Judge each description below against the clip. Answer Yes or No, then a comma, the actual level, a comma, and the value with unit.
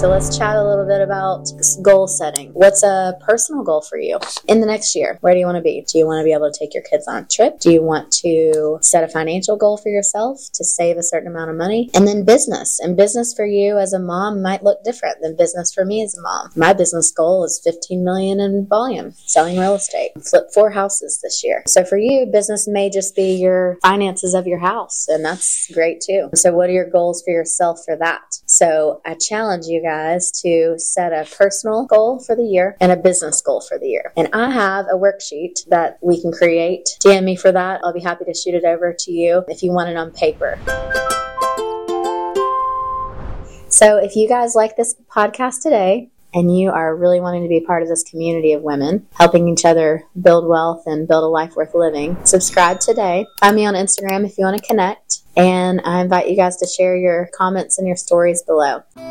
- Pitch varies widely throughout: No, average, 3.4 semitones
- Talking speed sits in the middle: No, fast, 225 wpm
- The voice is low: No, medium, 180 Hz